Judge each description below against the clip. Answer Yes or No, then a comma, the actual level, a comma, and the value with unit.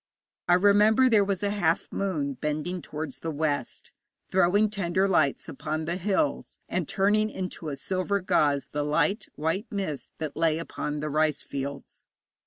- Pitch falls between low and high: Yes, medium, 170 Hz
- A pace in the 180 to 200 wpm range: No, average, 160 wpm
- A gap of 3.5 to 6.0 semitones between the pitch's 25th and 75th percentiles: Yes, average, 4.7 semitones